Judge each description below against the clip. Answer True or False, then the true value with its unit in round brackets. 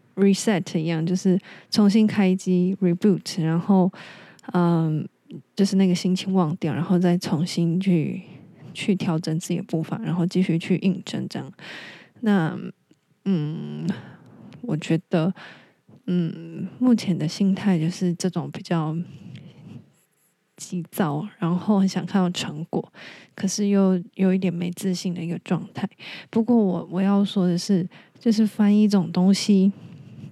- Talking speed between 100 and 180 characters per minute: False (220 characters per minute)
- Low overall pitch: False (185 Hz)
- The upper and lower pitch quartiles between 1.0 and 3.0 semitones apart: True (2.5 semitones)